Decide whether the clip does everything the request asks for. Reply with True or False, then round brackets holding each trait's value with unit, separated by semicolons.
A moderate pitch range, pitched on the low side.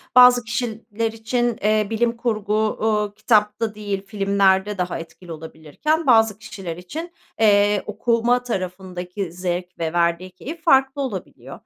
False (3.9 semitones; 210 Hz)